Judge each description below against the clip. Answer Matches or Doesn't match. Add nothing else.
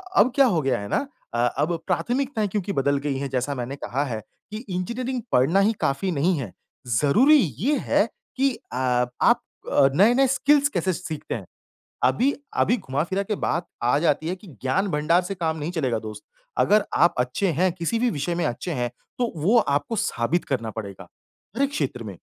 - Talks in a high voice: Doesn't match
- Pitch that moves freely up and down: Matches